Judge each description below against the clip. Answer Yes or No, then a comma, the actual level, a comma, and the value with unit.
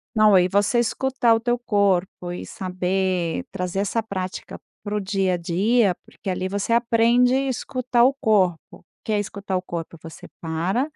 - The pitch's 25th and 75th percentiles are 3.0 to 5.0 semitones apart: Yes, average, 4.3 semitones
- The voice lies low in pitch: No, high, 200 Hz